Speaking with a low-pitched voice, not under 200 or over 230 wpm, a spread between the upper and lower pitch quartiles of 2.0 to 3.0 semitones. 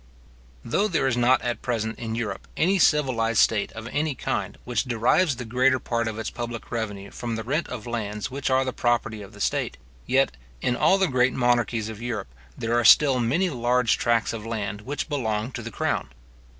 Yes: low, 120 Hz; fast, 205 wpm; narrow, 2.6 semitones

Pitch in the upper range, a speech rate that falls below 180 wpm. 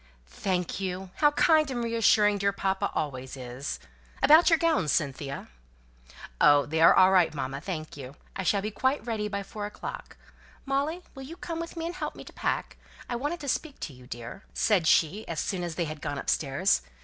No: high, 195 Hz; average, 195 wpm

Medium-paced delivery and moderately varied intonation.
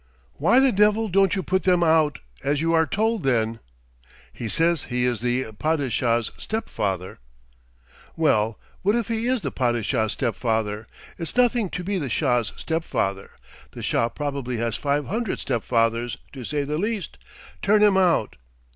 No: average, 170 wpm; wide, 8.5 semitones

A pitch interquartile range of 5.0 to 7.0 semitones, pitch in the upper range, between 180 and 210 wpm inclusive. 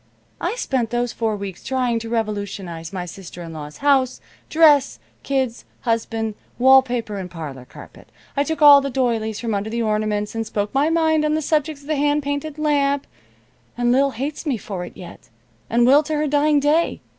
Yes: average, 5.3 semitones; high, 245 Hz; average, 190 wpm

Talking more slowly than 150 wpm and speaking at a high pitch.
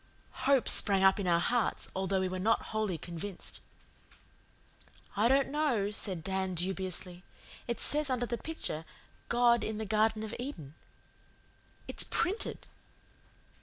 Yes: slow, 135 wpm; high, 210 Hz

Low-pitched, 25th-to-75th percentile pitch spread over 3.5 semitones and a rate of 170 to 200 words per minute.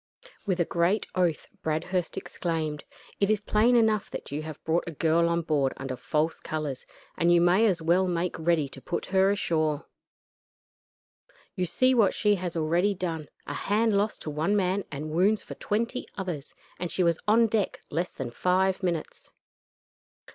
No: medium, 175 Hz; average, 4.0 semitones; average, 175 wpm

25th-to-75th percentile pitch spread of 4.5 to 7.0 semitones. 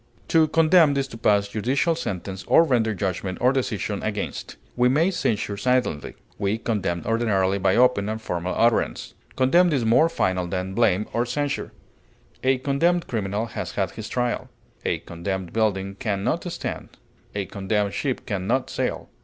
Yes: average, 4.8 semitones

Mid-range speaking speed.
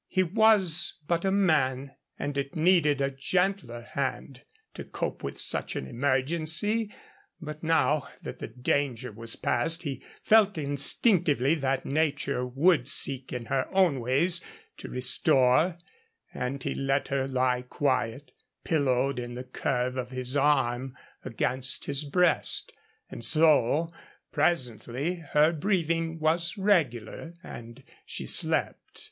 No: slow, 130 wpm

